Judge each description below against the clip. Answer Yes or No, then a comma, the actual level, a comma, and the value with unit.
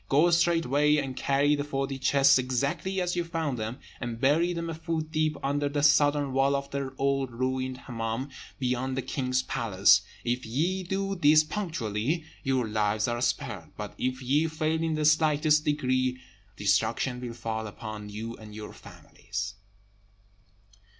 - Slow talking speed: No, average, 160 wpm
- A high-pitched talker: No, low, 135 Hz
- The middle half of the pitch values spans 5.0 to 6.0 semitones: No, average, 4.3 semitones